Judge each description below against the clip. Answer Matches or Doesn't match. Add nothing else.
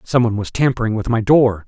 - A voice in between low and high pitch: Doesn't match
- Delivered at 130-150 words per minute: Doesn't match